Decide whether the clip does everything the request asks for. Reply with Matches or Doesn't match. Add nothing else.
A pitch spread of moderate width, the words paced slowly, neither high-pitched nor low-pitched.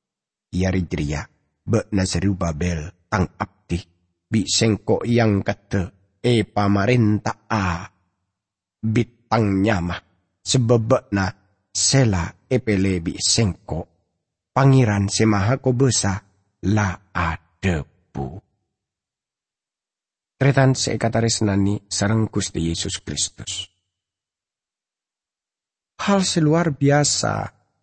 Doesn't match